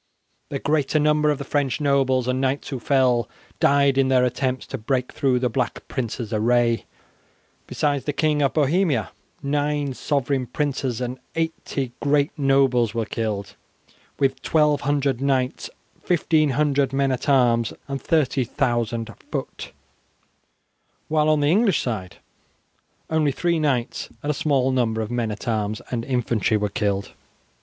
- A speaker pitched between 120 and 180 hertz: Yes, low, 135 Hz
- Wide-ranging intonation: No, average, 3.2 semitones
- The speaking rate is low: No, average, 145 wpm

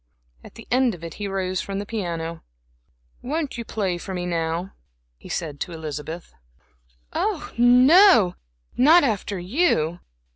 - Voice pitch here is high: Yes, high, 195 Hz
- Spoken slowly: No, average, 145 wpm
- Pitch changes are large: Yes, wide, 6.3 semitones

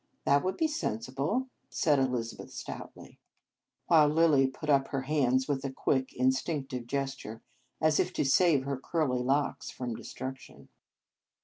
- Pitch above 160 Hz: No, low, 135 Hz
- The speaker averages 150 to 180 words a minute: No, average, 140 wpm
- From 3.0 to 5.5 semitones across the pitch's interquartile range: No, narrow, 2.6 semitones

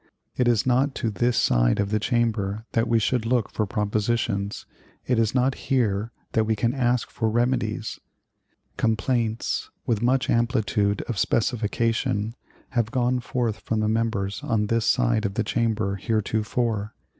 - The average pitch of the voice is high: No, low, 115 Hz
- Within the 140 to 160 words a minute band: Yes, average, 155 wpm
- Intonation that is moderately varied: No, narrow, 2.2 semitones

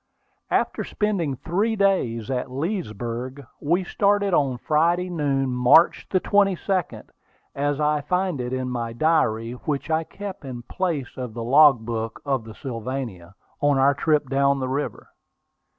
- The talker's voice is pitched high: No, medium, 140 Hz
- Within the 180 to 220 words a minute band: No, average, 140 wpm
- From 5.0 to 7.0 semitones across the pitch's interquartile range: Yes, wide, 5.5 semitones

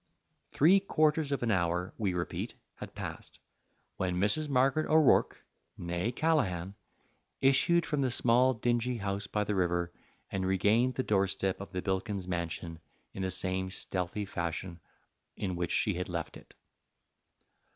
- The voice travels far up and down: Yes, wide, 5.8 semitones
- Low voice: Yes, low, 100 Hz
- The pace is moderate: Yes, average, 145 wpm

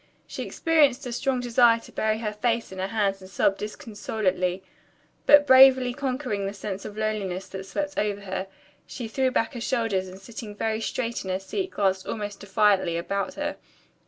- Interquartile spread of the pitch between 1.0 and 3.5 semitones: No, average, 4.2 semitones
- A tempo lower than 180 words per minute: No, average, 185 wpm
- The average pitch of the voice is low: No, high, 215 Hz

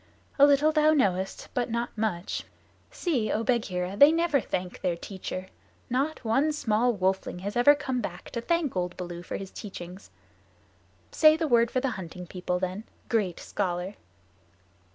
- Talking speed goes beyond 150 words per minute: Yes, average, 160 wpm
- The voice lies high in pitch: Yes, high, 220 Hz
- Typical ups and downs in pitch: No, wide, 6.8 semitones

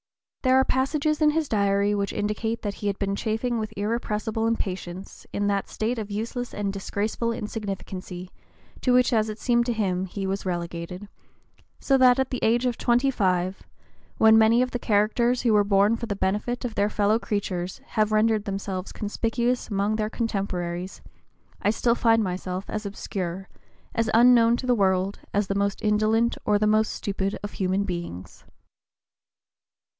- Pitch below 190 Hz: No, high, 210 Hz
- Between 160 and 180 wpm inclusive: Yes, average, 170 wpm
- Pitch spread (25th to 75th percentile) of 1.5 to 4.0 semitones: Yes, average, 2.9 semitones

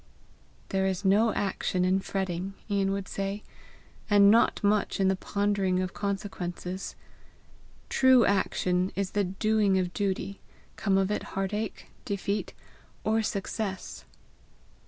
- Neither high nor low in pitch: No, high, 195 Hz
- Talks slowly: Yes, slow, 125 wpm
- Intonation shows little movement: Yes, narrow, 1.4 semitones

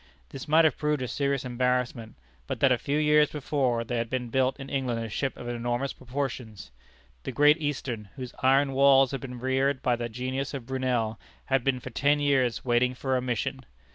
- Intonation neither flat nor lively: No, narrow, 2.3 semitones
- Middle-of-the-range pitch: No, low, 130 Hz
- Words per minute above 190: Yes, average, 200 wpm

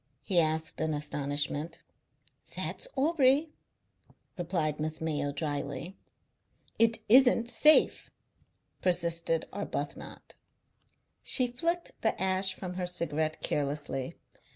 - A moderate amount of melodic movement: No, wide, 6.7 semitones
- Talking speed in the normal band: No, slow, 95 wpm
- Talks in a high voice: No, medium, 170 Hz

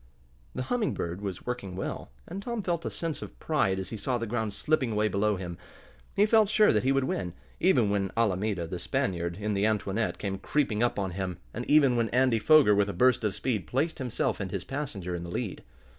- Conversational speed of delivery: No, fast, 225 wpm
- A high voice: No, low, 110 Hz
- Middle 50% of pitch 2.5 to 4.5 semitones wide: No, wide, 5.5 semitones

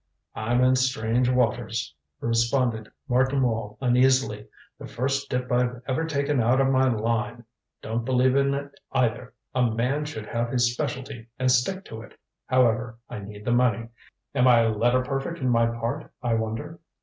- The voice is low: Yes, low, 125 Hz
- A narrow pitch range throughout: Yes, narrow, 2.1 semitones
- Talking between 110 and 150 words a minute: No, average, 165 wpm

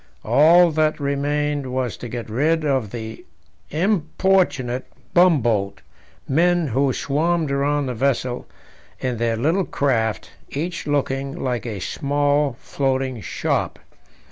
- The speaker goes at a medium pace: No, slow, 115 wpm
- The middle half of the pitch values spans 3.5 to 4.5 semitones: Yes, average, 3.8 semitones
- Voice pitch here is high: No, medium, 140 Hz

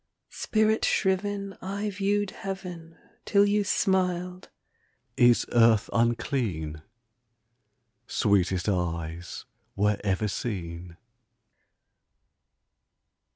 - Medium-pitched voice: No, low, 125 Hz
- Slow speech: Yes, slow, 70 wpm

